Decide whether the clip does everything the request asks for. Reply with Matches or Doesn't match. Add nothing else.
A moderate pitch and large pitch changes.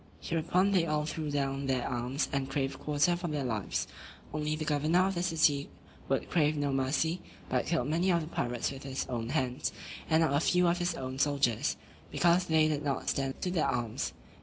Doesn't match